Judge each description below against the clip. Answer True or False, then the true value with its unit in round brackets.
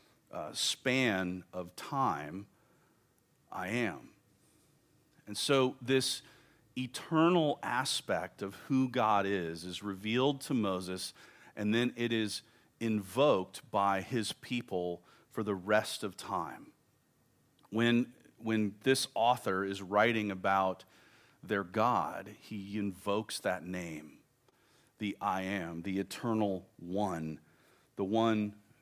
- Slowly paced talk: True (110 wpm)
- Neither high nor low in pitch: False (105 Hz)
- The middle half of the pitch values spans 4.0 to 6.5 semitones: True (4.3 semitones)